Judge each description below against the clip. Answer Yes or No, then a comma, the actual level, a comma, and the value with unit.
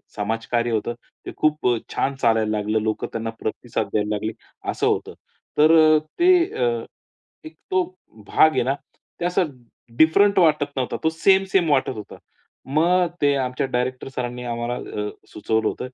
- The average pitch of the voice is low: Yes, low, 130 Hz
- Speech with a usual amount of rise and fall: No, wide, 5.9 semitones